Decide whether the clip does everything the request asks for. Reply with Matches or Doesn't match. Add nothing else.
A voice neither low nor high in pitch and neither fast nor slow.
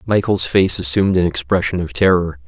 Doesn't match